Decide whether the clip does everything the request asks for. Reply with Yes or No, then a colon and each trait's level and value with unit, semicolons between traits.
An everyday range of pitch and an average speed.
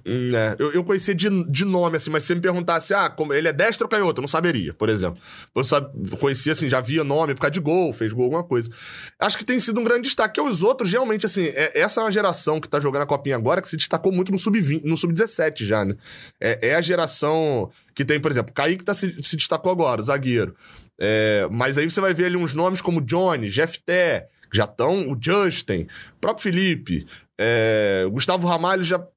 No: average, 4.9 semitones; fast, 230 wpm